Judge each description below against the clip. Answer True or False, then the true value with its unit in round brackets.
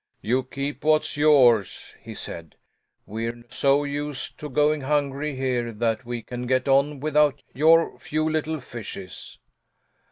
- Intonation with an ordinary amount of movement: True (3.6 semitones)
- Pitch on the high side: False (140 Hz)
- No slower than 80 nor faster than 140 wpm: True (135 wpm)